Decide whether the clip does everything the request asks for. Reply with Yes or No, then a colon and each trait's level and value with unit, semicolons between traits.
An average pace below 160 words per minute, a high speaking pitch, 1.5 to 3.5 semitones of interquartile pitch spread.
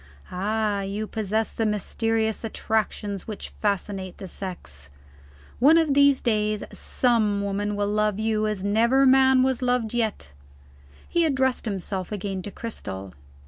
Yes: average, 140 wpm; high, 215 Hz; average, 2.8 semitones